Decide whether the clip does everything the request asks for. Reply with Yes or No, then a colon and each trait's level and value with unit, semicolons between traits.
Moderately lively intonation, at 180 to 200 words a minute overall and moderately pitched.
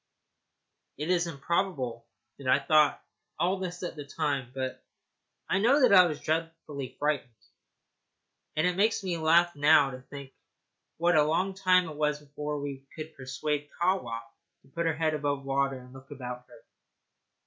No: average, 4.0 semitones; average, 165 wpm; medium, 150 Hz